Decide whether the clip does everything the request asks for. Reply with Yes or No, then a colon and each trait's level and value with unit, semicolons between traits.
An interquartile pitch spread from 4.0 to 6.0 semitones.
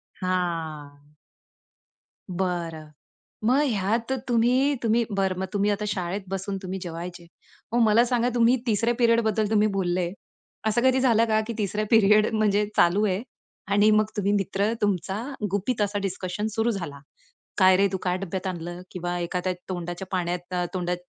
No: average, 3.4 semitones